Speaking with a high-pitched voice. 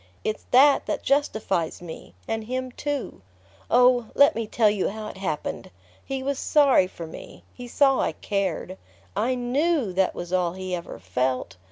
Yes: high, 215 Hz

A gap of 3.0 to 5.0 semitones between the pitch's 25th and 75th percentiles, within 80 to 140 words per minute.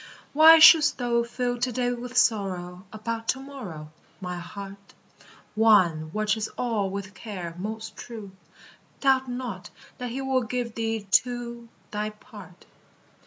Yes: average, 3.7 semitones; slow, 135 wpm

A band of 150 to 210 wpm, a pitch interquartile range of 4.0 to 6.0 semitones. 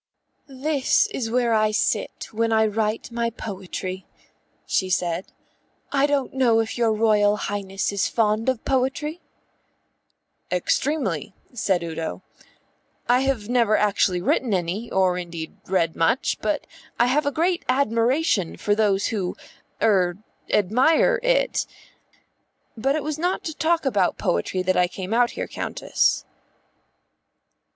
No: slow, 135 wpm; wide, 5.6 semitones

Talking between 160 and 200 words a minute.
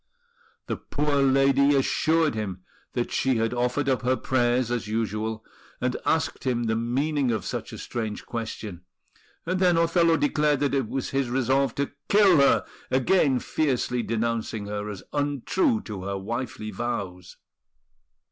No: average, 150 wpm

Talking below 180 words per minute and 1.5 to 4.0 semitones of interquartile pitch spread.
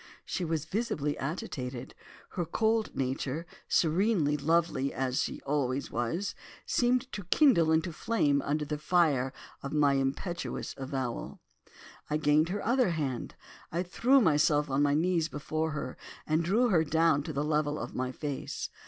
Yes: average, 155 wpm; average, 3.7 semitones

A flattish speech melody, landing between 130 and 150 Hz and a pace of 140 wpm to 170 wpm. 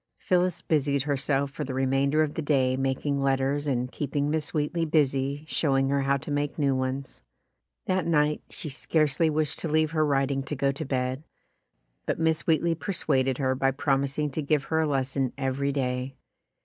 No: narrow, 2.2 semitones; medium, 140 Hz; average, 190 wpm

